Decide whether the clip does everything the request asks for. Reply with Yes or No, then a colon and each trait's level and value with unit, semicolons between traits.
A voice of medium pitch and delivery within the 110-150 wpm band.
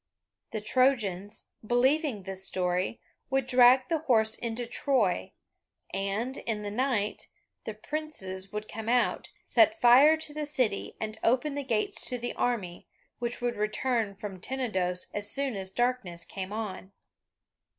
No: high, 225 Hz; average, 145 wpm